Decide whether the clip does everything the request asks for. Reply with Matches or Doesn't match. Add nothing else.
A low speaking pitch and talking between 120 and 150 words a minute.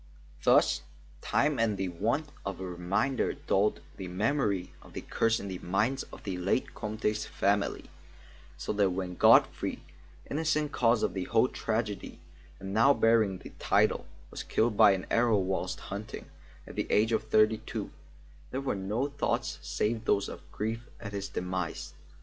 Doesn't match